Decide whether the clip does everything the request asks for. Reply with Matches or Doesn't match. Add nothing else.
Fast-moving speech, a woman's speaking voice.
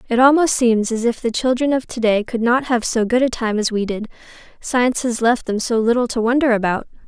Matches